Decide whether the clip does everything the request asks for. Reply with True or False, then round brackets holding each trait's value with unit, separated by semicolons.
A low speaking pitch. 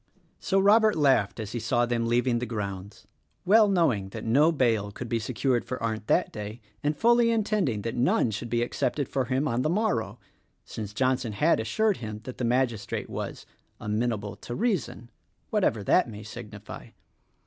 True (120 Hz)